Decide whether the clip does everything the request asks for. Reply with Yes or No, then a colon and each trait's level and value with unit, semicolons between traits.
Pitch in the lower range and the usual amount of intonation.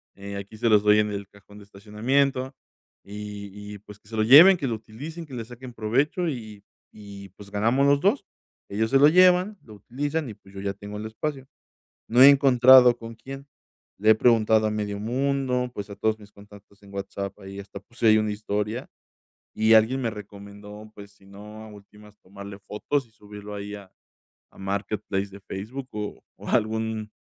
Yes: low, 105 Hz; average, 3.5 semitones